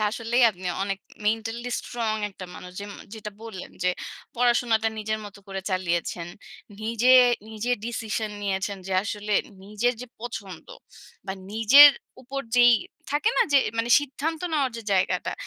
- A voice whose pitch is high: Yes, high, 220 Hz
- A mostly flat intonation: No, average, 3.4 semitones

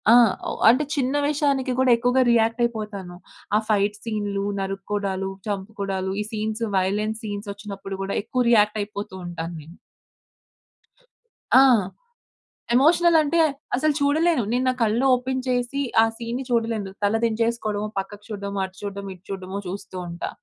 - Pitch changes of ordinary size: Yes, average, 3.7 semitones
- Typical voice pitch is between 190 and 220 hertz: Yes, high, 215 Hz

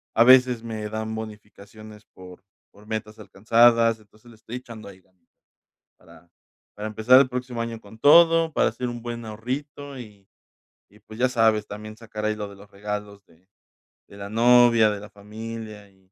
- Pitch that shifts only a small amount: Yes, narrow, 2.2 semitones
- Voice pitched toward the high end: No, low, 110 Hz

